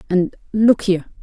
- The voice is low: No, high, 195 Hz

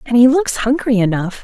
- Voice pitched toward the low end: No, high, 235 Hz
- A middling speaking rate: No, fast, 210 wpm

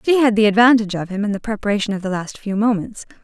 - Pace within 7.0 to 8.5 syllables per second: Yes, 7.1 syllables/s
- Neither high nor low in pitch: No, high, 210 Hz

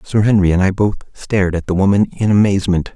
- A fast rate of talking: Yes, fast, 225 wpm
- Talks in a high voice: No, low, 100 Hz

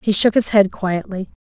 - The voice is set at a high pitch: Yes, high, 200 Hz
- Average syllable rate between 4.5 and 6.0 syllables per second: Yes, 4.9 syllables/s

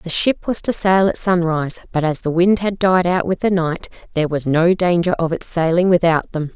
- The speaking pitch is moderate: Yes, medium, 175 Hz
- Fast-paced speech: Yes, fast, 240 wpm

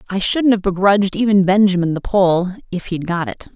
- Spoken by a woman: Yes, female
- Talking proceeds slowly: No, fast, 205 wpm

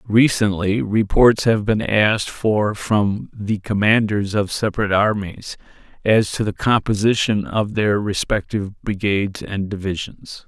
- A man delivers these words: Yes, male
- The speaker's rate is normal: No, slow, 125 wpm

